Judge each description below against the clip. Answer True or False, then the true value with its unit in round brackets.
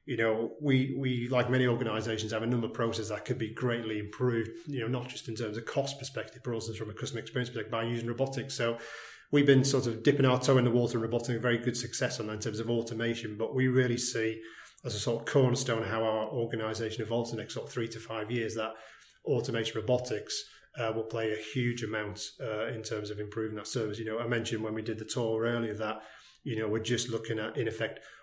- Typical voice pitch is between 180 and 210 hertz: False (115 Hz)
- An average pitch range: False (1.9 semitones)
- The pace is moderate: False (245 wpm)